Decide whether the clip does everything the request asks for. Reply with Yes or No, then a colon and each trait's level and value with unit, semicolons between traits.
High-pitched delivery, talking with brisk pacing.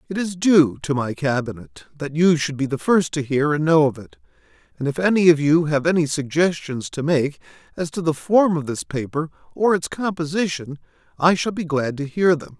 No: medium, 155 Hz; fast, 215 wpm